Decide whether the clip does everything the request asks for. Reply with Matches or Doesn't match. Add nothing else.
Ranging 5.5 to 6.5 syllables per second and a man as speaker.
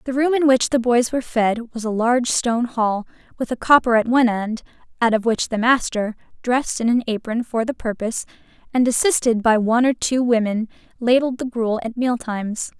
Doesn't match